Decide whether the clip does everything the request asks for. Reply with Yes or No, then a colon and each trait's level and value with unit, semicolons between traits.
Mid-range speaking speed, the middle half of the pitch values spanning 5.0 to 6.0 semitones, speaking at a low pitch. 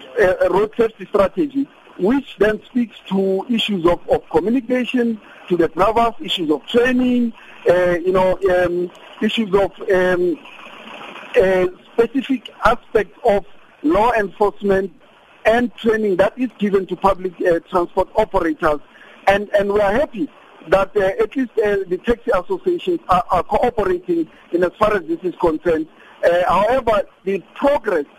No: average, 145 wpm; average, 5.3 semitones; high, 205 Hz